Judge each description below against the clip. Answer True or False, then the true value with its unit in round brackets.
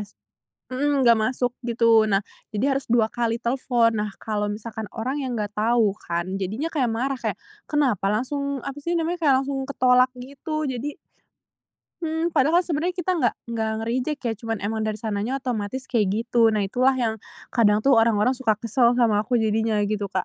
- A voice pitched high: True (235 Hz)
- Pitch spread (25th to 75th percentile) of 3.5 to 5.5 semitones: True (3.8 semitones)